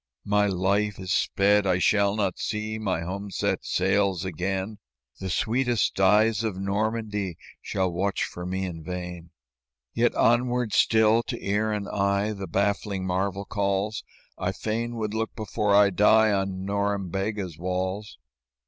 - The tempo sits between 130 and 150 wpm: Yes, average, 145 wpm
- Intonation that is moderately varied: No, narrow, 2.2 semitones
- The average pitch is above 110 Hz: No, low, 100 Hz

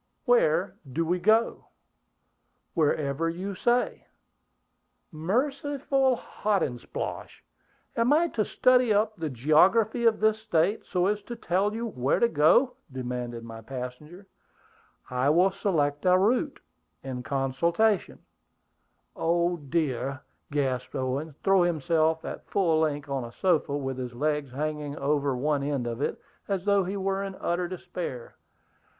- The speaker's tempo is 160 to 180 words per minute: No, slow, 135 wpm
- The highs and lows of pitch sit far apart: Yes, wide, 6.7 semitones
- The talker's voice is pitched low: No, medium, 165 Hz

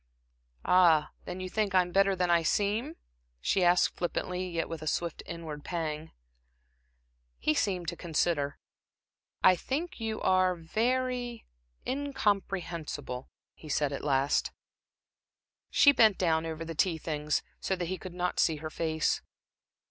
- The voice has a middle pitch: Yes, medium, 175 Hz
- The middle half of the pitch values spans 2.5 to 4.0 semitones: Yes, average, 3.6 semitones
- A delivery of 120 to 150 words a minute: Yes, average, 140 wpm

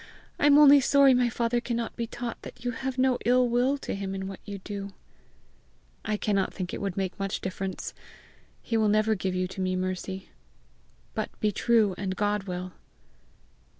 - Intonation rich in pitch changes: No, average, 4.0 semitones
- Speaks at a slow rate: No, average, 185 wpm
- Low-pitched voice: No, high, 210 Hz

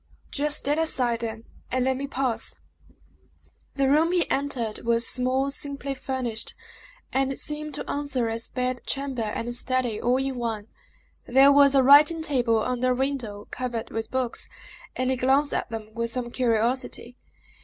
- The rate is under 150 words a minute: No, average, 160 wpm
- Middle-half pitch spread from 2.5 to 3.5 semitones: Yes, average, 2.9 semitones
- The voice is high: Yes, very high, 255 Hz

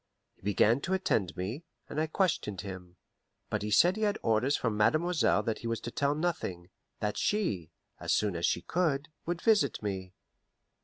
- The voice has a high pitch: No, low, 115 Hz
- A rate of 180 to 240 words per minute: Yes, average, 185 wpm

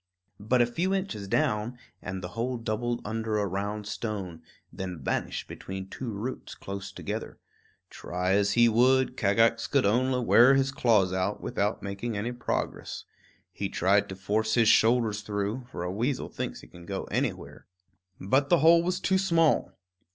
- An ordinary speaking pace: Yes, average, 165 wpm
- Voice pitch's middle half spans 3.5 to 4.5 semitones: Yes, average, 4.1 semitones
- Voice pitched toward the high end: No, low, 110 Hz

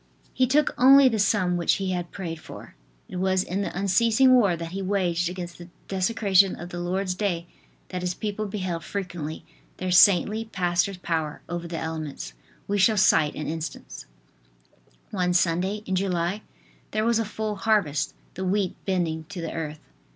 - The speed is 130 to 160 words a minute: No, average, 175 wpm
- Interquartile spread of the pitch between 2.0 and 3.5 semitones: Yes, average, 2.9 semitones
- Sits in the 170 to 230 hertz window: Yes, medium, 185 Hz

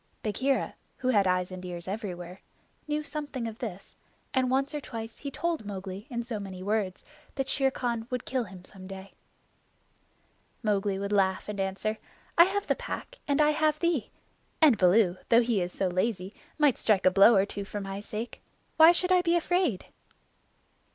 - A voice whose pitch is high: Yes, high, 220 Hz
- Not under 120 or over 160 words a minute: No, average, 185 wpm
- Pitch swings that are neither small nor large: No, wide, 6.1 semitones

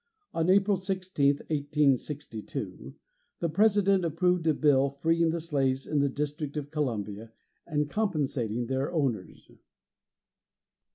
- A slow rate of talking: Yes, slow, 115 wpm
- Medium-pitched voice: Yes, medium, 150 Hz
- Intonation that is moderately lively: Yes, average, 3.8 semitones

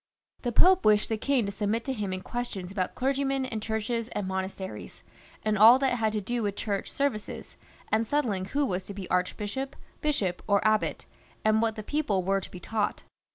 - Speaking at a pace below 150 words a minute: No, average, 200 wpm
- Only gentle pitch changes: No, average, 3.7 semitones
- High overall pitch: Yes, high, 215 Hz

